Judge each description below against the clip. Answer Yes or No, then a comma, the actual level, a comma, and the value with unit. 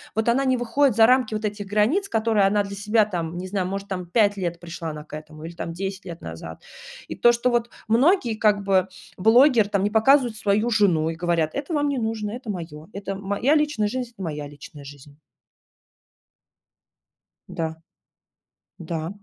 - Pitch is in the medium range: No, high, 205 Hz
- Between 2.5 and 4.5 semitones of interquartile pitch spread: No, average, 5.3 semitones